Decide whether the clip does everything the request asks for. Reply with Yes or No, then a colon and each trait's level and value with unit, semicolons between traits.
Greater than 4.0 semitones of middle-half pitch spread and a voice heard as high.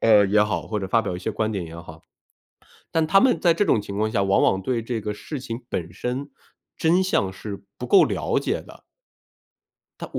No: average, 5.0 semitones; low, 110 Hz